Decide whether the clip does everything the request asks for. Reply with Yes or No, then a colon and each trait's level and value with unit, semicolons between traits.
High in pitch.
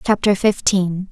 Yes: high, 195 Hz